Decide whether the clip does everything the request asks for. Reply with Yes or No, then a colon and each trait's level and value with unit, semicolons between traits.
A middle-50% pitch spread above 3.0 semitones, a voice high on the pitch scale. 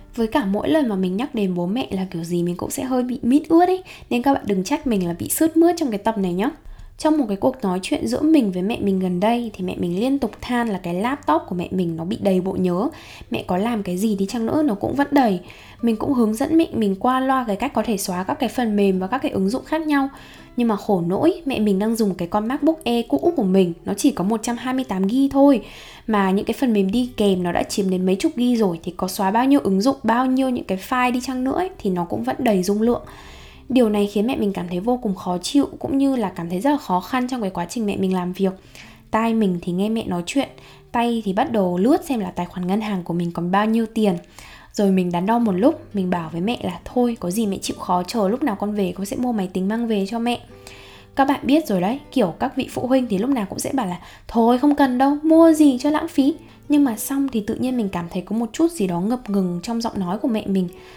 Yes: wide, 5.6 semitones; high, 220 Hz